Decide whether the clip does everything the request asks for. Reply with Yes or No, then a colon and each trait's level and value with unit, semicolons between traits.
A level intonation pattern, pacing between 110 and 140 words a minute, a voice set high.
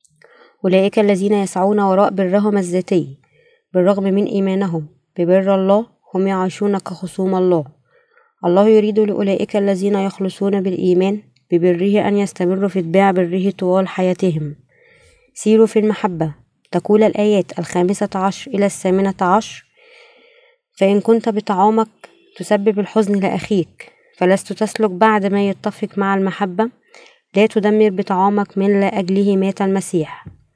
Yes: narrow, 2.1 semitones; average, 120 wpm; high, 200 Hz